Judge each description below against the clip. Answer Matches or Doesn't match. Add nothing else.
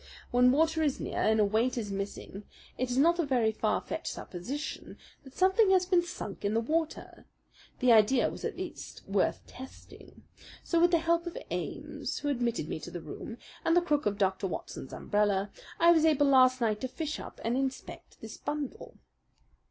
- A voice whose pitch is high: Matches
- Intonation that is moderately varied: Doesn't match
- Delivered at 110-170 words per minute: Doesn't match